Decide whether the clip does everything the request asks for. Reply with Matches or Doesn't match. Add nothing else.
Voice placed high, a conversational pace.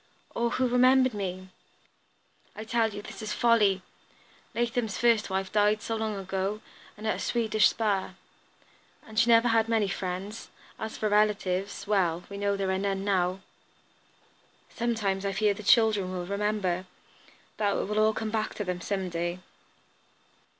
Matches